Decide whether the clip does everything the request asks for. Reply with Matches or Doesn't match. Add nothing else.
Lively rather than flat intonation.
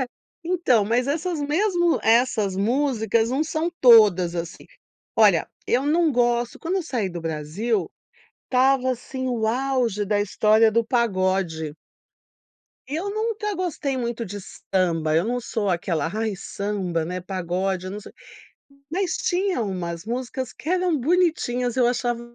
Matches